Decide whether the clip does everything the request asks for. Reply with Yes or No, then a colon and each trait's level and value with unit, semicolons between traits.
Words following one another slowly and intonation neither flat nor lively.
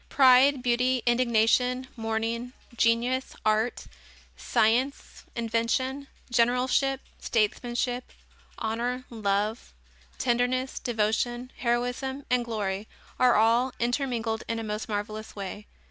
No: slow, 95 wpm; narrow, 2.2 semitones